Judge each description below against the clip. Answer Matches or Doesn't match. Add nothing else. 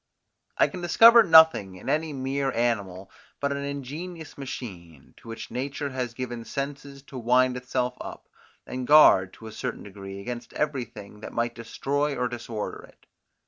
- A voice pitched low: Matches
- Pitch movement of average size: Matches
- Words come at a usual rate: Matches